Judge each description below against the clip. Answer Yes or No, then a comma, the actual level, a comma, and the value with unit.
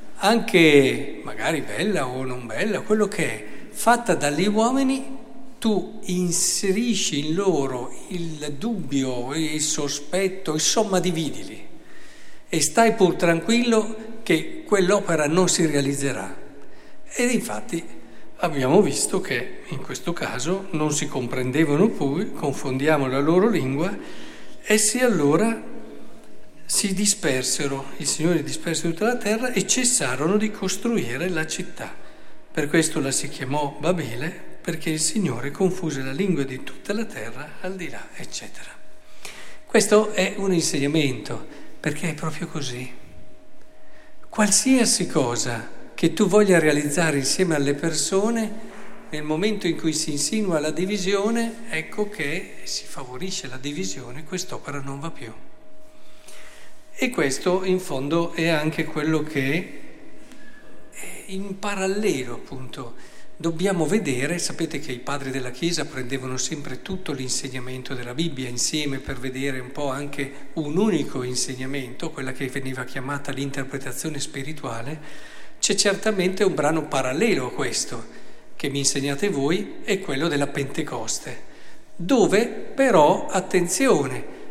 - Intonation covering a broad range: Yes, wide, 6.0 semitones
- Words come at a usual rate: Yes, average, 125 wpm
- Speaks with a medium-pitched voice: Yes, medium, 160 Hz